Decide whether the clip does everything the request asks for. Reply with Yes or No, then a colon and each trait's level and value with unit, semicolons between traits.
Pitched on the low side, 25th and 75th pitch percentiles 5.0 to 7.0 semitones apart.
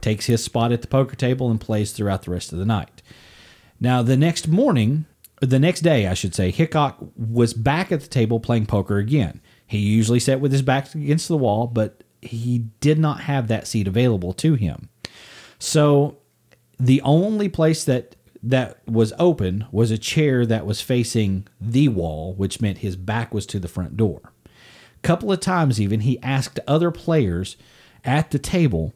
Yes: low, 120 Hz; average, 5.3 semitones